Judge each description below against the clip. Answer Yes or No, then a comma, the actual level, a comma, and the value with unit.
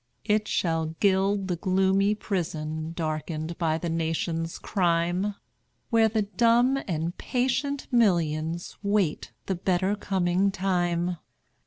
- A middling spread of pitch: Yes, average, 3.7 semitones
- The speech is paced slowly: Yes, slow, 115 wpm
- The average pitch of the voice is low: No, medium, 180 Hz